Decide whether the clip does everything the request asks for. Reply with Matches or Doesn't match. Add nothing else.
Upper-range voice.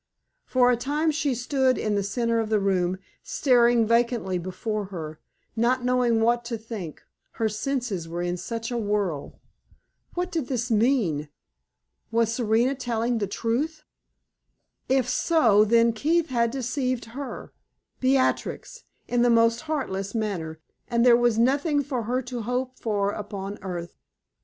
Matches